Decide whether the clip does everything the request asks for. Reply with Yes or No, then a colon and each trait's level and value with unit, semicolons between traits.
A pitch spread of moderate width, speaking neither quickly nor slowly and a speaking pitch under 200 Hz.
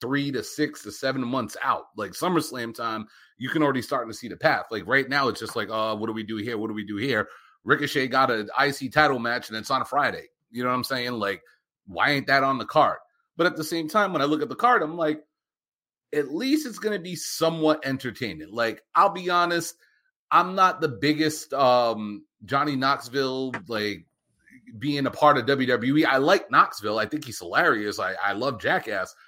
No: average, 4.6 semitones; fast, 215 wpm; medium, 140 Hz